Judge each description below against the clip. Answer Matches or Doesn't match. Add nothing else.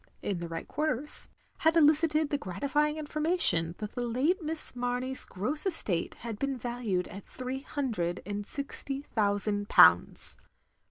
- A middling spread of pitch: Doesn't match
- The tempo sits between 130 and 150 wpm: Matches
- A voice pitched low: Doesn't match